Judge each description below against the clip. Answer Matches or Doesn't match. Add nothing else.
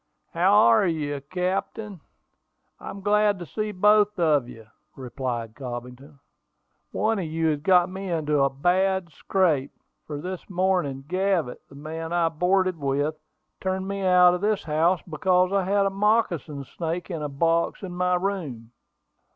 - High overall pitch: Doesn't match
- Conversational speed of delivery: Matches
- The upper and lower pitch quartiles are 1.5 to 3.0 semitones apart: Doesn't match